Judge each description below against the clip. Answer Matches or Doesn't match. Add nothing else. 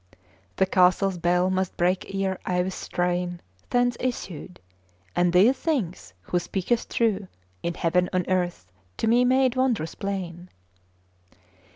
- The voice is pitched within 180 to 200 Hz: Matches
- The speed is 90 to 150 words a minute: Matches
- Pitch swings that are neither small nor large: Matches